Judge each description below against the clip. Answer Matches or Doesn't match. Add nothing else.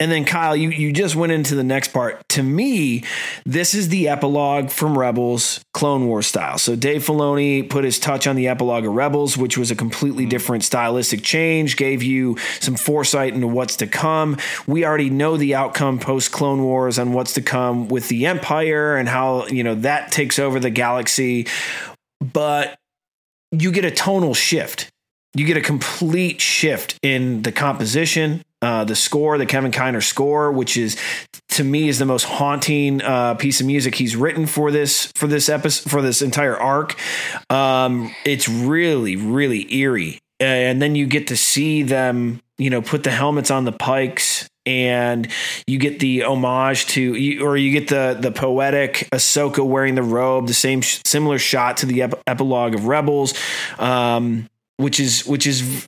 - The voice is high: Doesn't match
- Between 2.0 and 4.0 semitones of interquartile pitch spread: Matches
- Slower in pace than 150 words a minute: Doesn't match